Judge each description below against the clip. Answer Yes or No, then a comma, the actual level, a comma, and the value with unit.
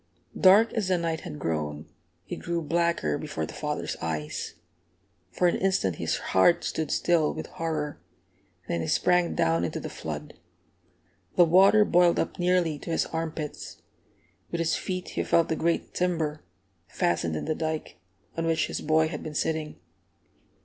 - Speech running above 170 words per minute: No, average, 165 wpm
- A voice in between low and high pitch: Yes, medium, 160 Hz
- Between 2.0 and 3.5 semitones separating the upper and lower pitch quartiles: Yes, average, 3.0 semitones